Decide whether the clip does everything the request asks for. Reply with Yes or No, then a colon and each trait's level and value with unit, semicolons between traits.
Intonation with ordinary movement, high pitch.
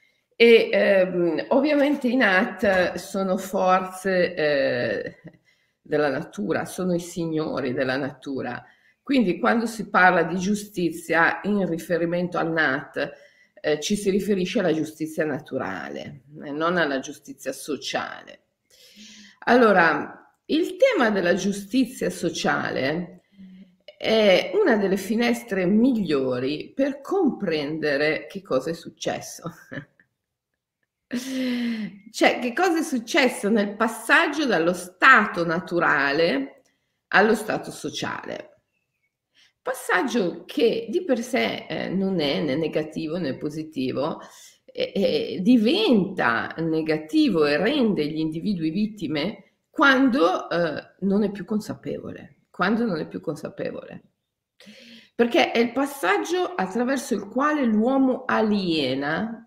No: wide, 7.1 semitones; high, 195 Hz